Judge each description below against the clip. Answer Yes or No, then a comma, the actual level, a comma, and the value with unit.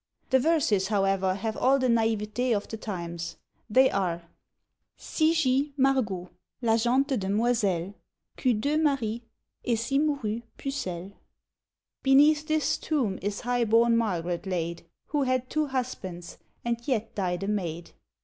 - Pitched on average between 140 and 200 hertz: No, high, 230 Hz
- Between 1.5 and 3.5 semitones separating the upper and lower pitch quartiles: No, wide, 5.6 semitones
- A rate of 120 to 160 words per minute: Yes, average, 140 wpm